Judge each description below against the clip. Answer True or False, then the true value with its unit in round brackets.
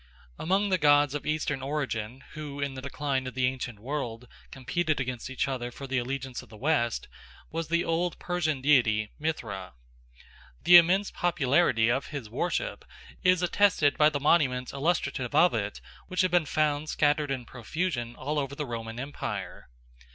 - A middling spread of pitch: True (3.8 semitones)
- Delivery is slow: False (165 wpm)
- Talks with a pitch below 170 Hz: True (140 Hz)